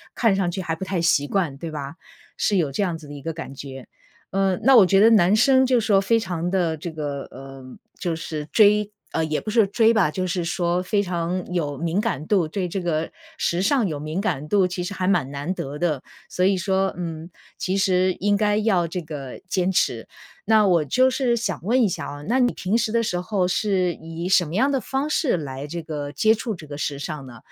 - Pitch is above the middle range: No, medium, 180 Hz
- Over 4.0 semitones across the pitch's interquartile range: Yes, average, 4.6 semitones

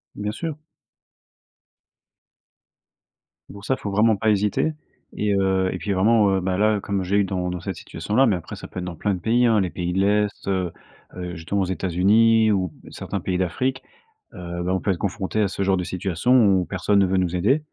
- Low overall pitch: Yes, very low, 95 Hz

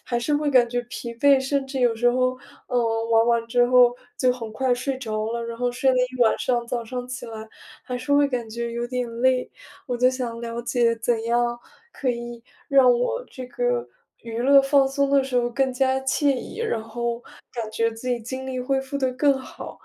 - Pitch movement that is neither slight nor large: No, narrow, 2.0 semitones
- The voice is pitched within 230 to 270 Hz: Yes, very high, 250 Hz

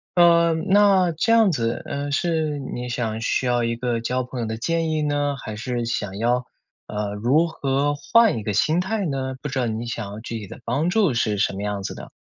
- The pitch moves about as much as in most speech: No, wide, 5.8 semitones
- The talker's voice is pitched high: No, low, 130 Hz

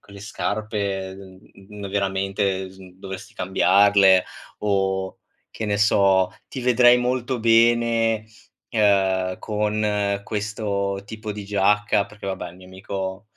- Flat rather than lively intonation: Yes, narrow, 2.0 semitones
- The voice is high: No, low, 100 Hz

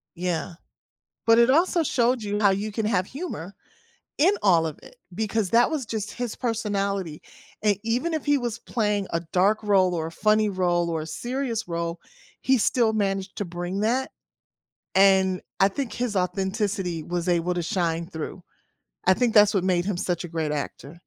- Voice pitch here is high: Yes, high, 200 Hz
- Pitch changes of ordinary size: Yes, average, 4.3 semitones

